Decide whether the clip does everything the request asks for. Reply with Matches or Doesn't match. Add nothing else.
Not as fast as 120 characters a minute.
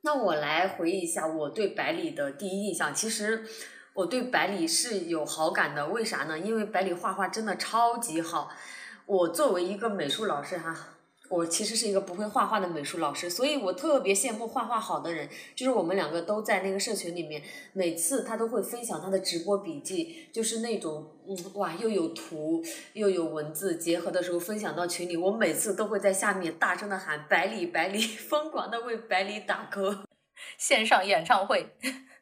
Doesn't match